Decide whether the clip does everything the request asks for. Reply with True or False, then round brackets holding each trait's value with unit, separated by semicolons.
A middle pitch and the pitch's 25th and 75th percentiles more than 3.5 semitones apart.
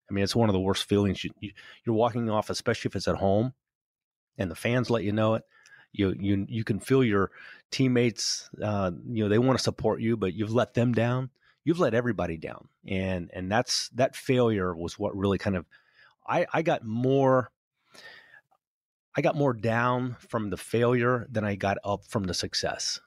False (110 Hz; 3.9 semitones)